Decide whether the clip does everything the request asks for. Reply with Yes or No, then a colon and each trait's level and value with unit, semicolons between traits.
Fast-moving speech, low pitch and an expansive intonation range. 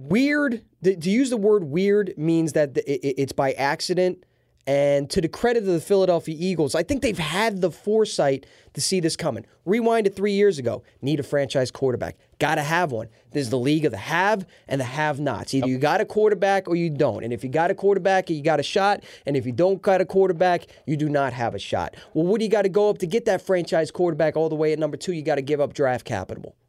No: fast, 245 wpm; medium, 160 Hz; wide, 5.7 semitones